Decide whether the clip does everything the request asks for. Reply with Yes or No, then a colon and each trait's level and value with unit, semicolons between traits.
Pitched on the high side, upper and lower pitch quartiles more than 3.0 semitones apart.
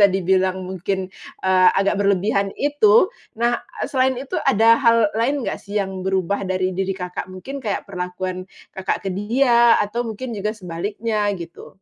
Yes: high, 200 Hz; average, 3.6 semitones